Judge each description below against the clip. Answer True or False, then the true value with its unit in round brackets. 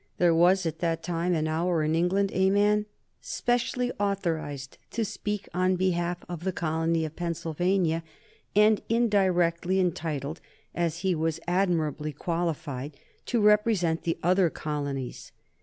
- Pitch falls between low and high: True (175 Hz)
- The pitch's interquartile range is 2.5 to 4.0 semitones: True (2.9 semitones)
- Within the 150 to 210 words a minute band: False (135 wpm)